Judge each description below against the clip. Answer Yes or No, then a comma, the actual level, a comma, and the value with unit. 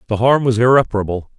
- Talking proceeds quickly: No, average, 175 wpm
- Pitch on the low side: Yes, low, 115 Hz